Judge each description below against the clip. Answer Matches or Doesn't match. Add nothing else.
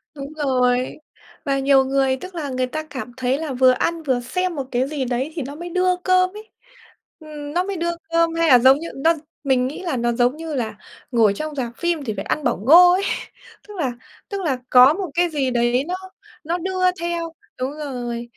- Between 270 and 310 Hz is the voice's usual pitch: Matches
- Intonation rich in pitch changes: Doesn't match